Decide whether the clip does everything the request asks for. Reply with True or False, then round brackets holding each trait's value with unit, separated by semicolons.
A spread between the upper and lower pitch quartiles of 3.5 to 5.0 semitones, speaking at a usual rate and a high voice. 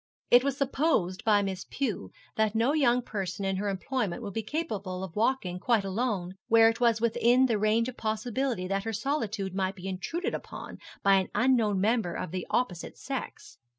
True (4.2 semitones; 185 wpm; 215 Hz)